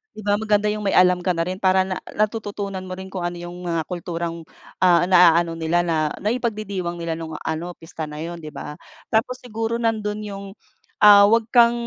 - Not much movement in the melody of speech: No, average, 3.6 semitones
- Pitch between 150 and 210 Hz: Yes, medium, 185 Hz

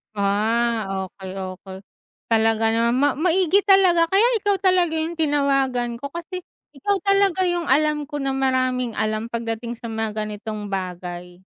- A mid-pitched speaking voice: No, high, 245 Hz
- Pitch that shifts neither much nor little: No, wide, 7.1 semitones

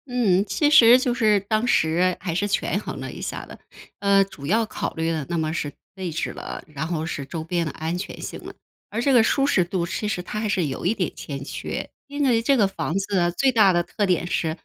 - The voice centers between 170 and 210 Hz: Yes, high, 190 Hz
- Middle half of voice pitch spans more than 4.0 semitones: Yes, average, 4.9 semitones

